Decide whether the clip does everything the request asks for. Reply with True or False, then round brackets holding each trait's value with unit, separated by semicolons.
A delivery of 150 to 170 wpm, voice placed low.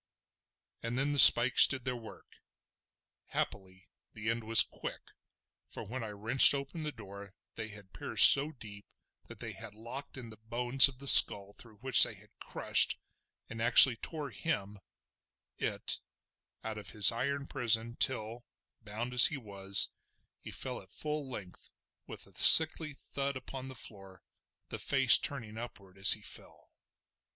True (155 wpm; 115 Hz)